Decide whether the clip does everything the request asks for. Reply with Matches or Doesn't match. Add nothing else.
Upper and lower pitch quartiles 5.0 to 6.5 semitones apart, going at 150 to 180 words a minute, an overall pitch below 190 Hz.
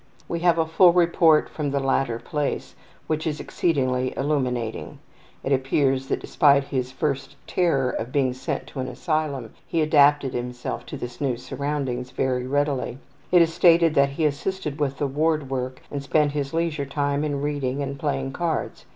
Doesn't match